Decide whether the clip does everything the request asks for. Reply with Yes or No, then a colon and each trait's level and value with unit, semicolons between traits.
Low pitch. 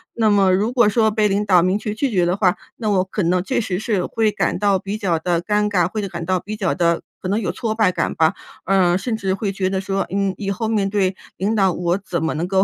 No: high, 195 Hz